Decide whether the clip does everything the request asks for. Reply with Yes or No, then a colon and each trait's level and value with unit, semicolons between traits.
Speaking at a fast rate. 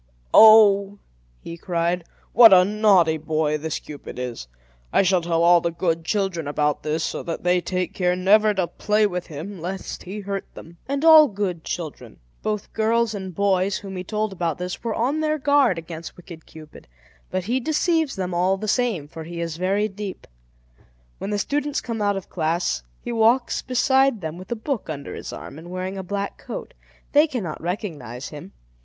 No: average, 190 wpm